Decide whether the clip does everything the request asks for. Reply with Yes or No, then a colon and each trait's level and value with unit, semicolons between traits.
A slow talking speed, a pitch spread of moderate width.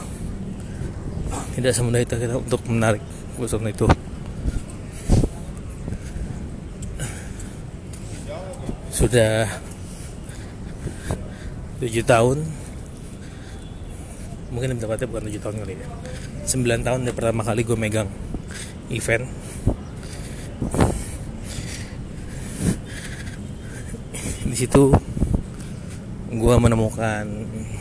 Yes: slow, 65 wpm; average, 3.7 semitones